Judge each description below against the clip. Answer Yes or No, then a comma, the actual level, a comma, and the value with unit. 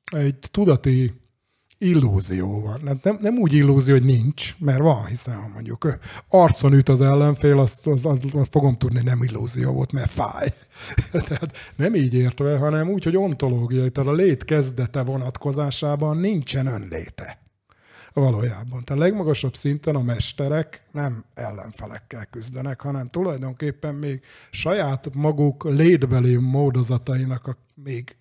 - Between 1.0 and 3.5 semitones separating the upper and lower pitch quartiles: Yes, average, 3.1 semitones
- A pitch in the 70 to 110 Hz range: No, low, 135 Hz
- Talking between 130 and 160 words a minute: Yes, average, 135 wpm